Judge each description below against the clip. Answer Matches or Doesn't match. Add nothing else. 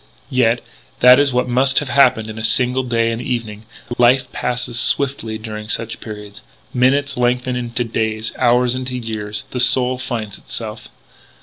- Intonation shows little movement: Matches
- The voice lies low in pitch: Matches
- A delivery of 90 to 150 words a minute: Doesn't match